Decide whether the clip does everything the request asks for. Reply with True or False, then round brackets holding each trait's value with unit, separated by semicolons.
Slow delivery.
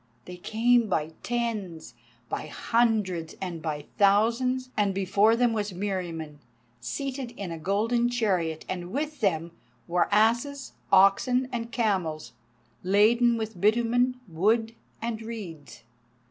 True (120 wpm)